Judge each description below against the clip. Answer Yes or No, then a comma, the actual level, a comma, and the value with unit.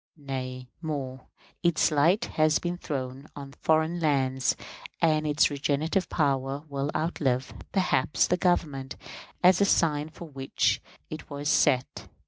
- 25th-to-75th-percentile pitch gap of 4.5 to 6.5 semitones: No, average, 3.0 semitones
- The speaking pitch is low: No, medium, 145 Hz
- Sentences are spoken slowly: Yes, slow, 130 wpm